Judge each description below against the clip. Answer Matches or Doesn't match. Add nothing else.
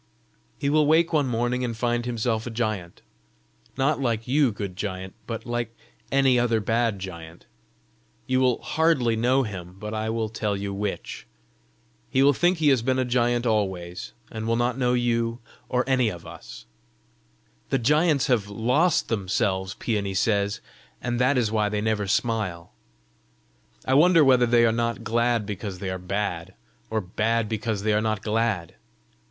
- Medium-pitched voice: Doesn't match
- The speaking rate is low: Doesn't match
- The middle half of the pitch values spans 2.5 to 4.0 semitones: Matches